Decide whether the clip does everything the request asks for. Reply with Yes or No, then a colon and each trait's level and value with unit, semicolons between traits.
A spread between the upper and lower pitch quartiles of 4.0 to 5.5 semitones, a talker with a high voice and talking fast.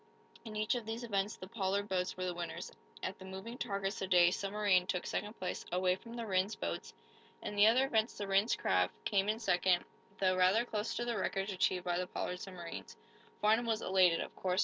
No: average, 2.9 semitones; high, 195 Hz; fast, 215 wpm